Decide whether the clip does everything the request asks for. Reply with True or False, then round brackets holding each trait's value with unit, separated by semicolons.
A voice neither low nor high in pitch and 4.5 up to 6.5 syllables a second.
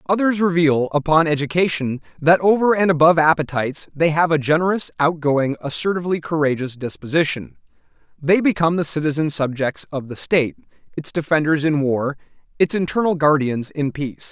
True (155 Hz; 5.7 syllables/s)